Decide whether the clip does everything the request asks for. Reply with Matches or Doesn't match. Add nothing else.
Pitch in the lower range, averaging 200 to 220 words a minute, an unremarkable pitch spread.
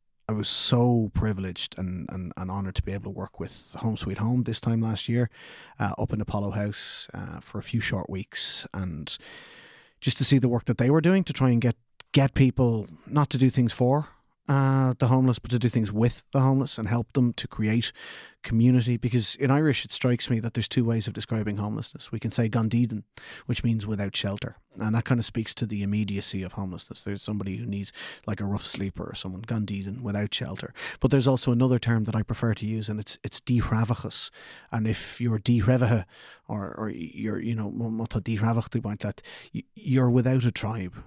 Matches